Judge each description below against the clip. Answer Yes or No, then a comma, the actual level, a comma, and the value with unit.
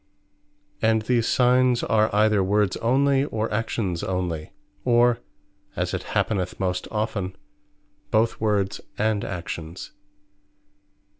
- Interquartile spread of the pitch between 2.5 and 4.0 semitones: Yes, average, 3.5 semitones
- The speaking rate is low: Yes, slow, 105 wpm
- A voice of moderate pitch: No, low, 110 Hz